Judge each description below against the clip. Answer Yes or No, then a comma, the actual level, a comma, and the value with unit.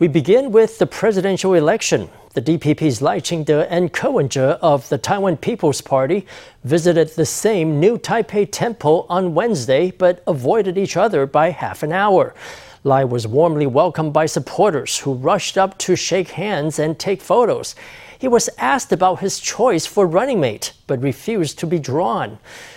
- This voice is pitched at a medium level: Yes, medium, 175 Hz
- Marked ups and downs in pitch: No, average, 4.3 semitones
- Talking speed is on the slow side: No, average, 165 wpm